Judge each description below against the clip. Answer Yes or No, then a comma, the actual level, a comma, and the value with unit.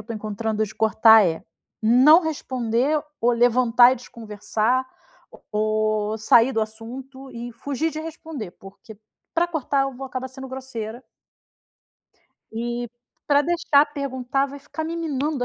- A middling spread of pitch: Yes, average, 4.0 semitones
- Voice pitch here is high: Yes, very high, 250 Hz